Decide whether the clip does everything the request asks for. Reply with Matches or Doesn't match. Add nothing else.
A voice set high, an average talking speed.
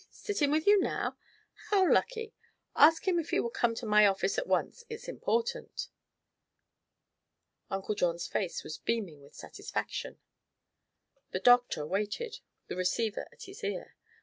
Matches